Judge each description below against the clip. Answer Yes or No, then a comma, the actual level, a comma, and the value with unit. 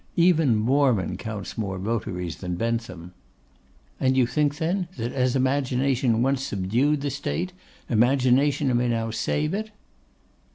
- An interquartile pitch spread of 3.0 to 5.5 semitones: Yes, average, 4.0 semitones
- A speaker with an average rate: No, slow, 130 wpm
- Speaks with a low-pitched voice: Yes, low, 125 Hz